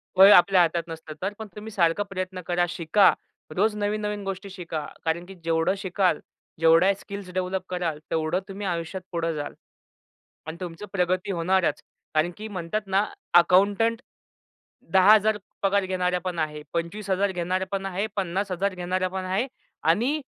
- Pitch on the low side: No, medium, 185 Hz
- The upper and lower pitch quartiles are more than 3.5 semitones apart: No, average, 2.7 semitones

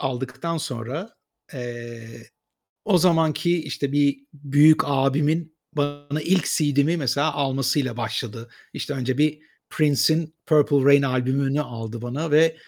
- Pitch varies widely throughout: No, average, 3.1 semitones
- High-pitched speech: No, medium, 145 Hz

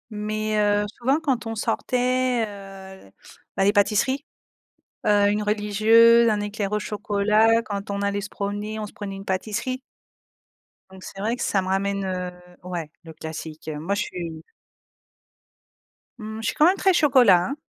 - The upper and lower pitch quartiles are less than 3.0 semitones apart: Yes, narrow, 2.5 semitones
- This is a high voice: Yes, high, 205 Hz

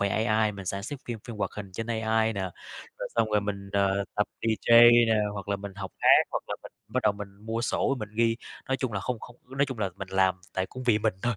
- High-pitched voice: No, low, 105 Hz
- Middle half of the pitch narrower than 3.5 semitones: Yes, narrow, 2.6 semitones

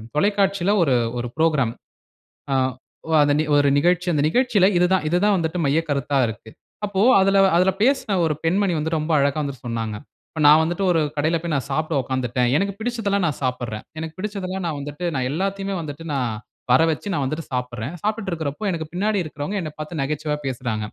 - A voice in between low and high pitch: Yes, medium, 160 Hz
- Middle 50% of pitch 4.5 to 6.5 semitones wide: Yes, average, 5.3 semitones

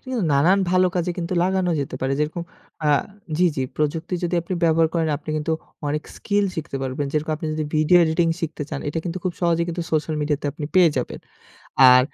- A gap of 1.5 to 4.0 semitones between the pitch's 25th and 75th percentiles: Yes, average, 2.9 semitones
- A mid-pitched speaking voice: Yes, medium, 160 Hz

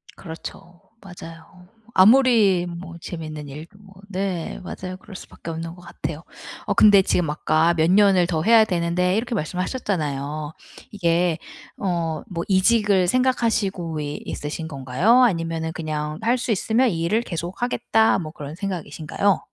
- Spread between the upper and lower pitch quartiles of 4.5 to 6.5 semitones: No, average, 3.7 semitones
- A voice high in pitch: No, medium, 175 Hz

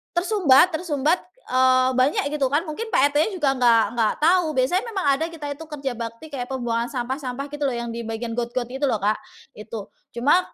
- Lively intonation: No, average, 4.1 semitones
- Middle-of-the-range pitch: No, very high, 265 Hz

